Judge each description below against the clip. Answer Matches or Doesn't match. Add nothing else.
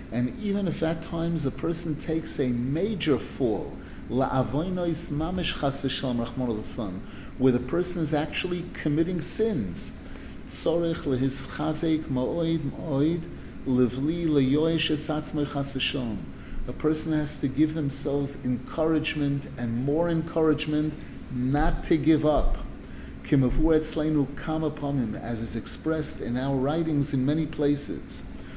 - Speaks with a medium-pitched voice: Matches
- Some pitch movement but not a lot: Matches